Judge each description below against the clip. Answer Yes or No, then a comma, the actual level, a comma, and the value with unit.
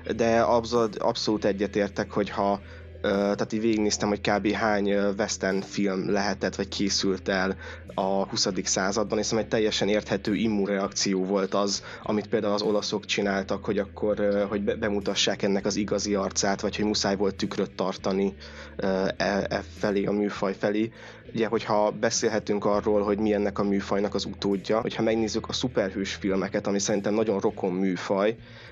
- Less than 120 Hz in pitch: Yes, low, 100 Hz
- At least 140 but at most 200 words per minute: Yes, fast, 155 wpm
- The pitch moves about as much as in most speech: No, narrow, 1.3 semitones